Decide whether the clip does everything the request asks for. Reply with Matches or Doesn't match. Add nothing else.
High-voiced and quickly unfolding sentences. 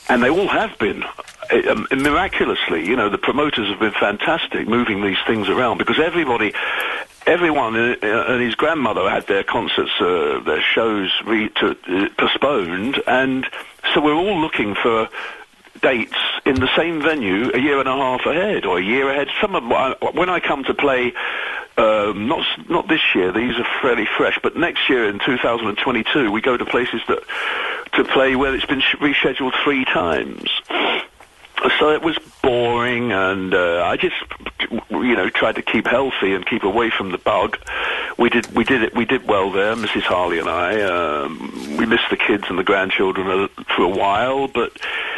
Doesn't match